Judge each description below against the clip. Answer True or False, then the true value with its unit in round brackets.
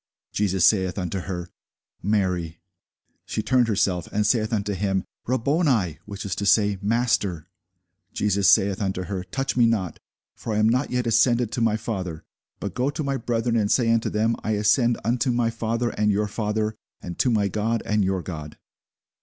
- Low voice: True (105 Hz)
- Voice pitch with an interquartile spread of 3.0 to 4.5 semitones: True (3.3 semitones)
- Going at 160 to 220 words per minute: True (180 wpm)